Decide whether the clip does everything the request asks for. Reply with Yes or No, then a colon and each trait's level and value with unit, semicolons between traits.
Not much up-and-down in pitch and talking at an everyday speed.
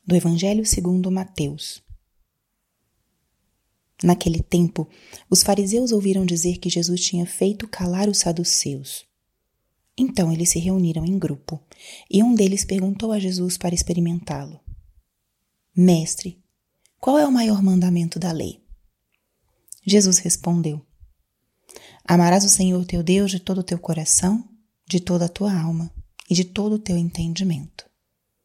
Yes: narrow, 2.3 semitones; average, 130 wpm